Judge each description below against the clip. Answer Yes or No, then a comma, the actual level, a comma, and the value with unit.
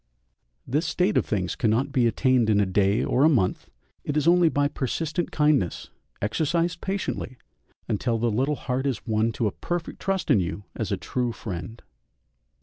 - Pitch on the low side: Yes, low, 130 Hz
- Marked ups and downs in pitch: Yes, wide, 5.9 semitones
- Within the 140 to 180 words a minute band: Yes, average, 175 wpm